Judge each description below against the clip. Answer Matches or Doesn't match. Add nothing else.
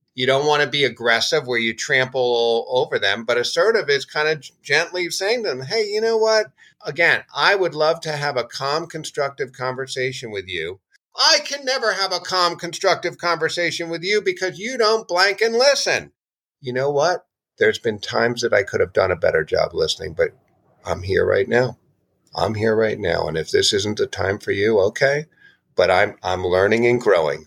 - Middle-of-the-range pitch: Matches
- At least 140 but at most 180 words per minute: Doesn't match